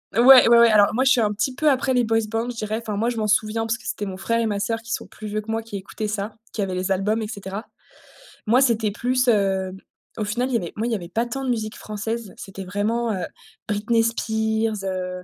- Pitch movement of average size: No, narrow, 2.2 semitones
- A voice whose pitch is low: No, high, 220 Hz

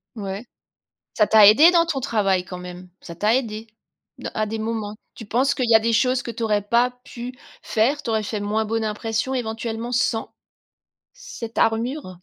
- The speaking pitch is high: Yes, high, 225 Hz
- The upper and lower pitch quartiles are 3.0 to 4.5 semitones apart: No, narrow, 2.5 semitones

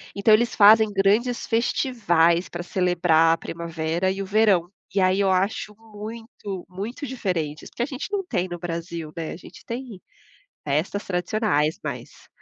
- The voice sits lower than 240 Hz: Yes, high, 190 Hz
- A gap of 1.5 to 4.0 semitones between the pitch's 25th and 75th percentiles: No, average, 4.5 semitones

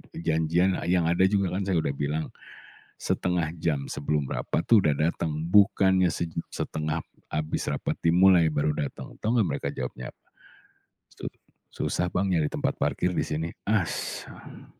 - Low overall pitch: Yes, very low, 85 Hz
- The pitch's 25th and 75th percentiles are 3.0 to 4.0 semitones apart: Yes, average, 3.4 semitones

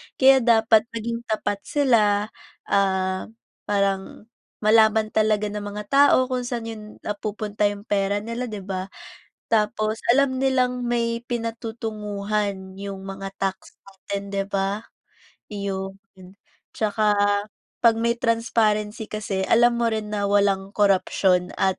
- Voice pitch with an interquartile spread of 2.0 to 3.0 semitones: Yes, narrow, 2.5 semitones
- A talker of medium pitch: No, high, 210 Hz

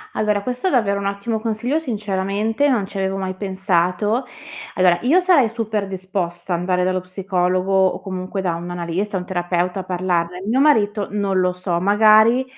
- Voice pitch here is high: Yes, high, 195 Hz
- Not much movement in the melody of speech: No, average, 3.0 semitones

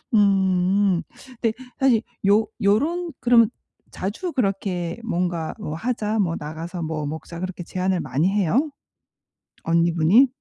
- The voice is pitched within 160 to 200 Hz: Yes, high, 190 Hz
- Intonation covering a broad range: No, average, 4.4 semitones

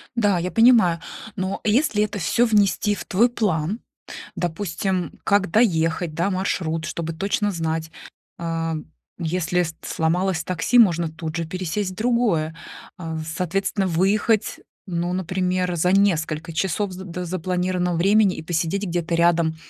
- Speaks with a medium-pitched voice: Yes, medium, 180 Hz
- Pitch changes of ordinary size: Yes, average, 3.3 semitones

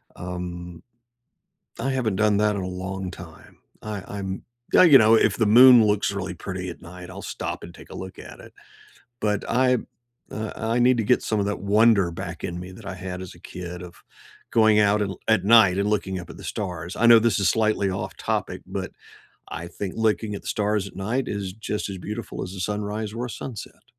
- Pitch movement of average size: Yes, average, 3.0 semitones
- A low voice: Yes, low, 100 Hz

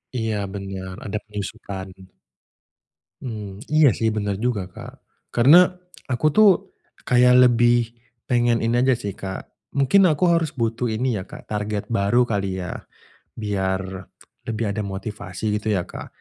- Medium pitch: No, low, 110 Hz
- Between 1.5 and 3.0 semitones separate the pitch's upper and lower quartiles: No, average, 3.7 semitones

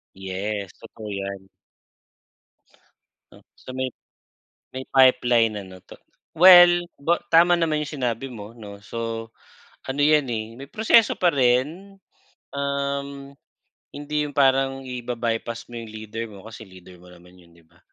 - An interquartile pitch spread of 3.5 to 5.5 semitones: Yes, average, 4.8 semitones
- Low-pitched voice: Yes, low, 125 Hz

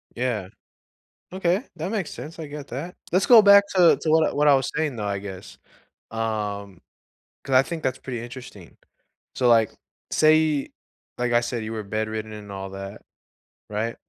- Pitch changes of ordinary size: No, wide, 6.6 semitones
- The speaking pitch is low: Yes, low, 120 Hz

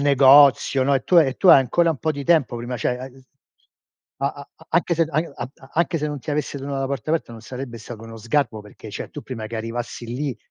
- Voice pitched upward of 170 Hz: No, low, 135 Hz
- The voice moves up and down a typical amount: Yes, average, 3.7 semitones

